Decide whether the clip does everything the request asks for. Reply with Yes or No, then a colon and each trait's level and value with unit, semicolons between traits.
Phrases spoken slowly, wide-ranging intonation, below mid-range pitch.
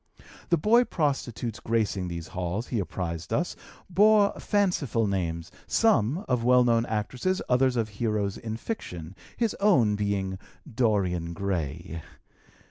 Yes: slow, 130 wpm; wide, 6.2 semitones; low, 110 Hz